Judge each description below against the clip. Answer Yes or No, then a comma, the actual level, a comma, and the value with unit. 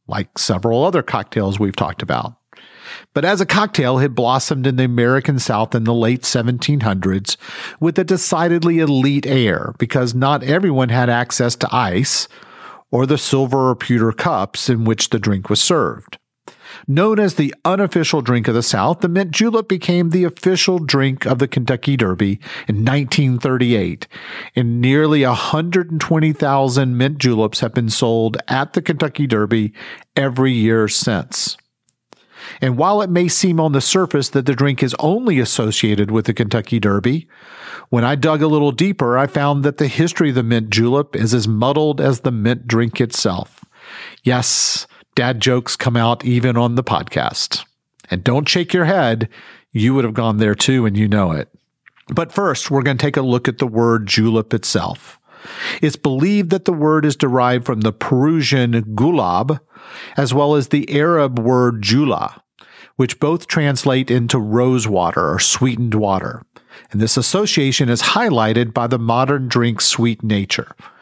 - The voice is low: Yes, low, 130 Hz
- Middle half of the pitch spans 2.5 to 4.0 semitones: No, average, 4.4 semitones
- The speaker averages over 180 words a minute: No, average, 165 wpm